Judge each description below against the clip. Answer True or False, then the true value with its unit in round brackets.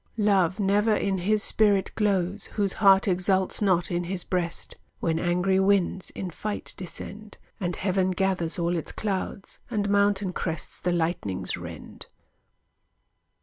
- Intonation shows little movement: True (2.3 semitones)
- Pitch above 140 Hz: True (190 Hz)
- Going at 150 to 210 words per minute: False (140 wpm)